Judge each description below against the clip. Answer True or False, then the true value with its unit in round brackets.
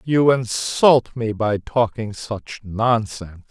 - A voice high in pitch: False (115 Hz)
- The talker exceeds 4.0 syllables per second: False (3.3 syllables/s)